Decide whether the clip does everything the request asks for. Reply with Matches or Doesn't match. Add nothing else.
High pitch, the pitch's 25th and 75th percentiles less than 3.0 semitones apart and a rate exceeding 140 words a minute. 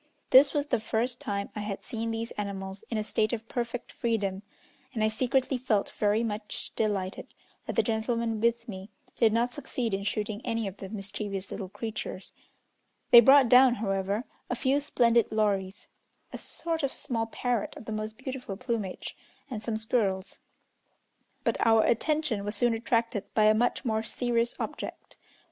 Matches